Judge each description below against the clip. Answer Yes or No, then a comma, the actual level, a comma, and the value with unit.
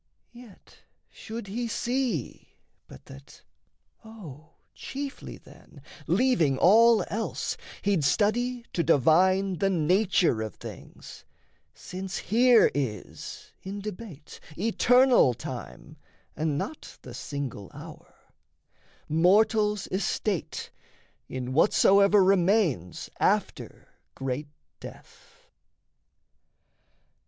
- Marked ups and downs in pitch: Yes, wide, 6.6 semitones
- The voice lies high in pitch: Yes, high, 195 Hz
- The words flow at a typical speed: No, slow, 90 wpm